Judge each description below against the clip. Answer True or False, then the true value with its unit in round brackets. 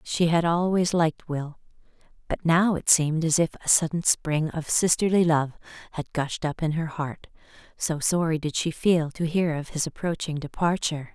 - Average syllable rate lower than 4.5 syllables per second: False (4.9 syllables/s)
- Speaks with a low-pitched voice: False (160 Hz)